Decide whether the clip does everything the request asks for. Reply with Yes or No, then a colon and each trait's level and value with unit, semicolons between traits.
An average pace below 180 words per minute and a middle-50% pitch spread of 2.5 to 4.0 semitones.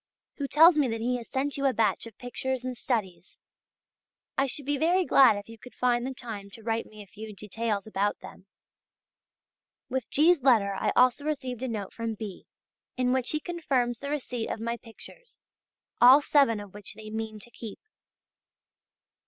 No: average, 185 wpm; average, 3.7 semitones